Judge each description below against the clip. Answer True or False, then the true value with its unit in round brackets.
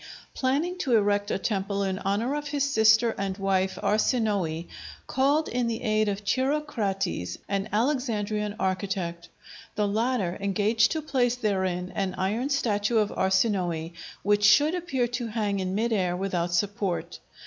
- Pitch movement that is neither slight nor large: True (4.0 semitones)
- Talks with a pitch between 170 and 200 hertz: False (210 Hz)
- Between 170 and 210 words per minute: False (150 wpm)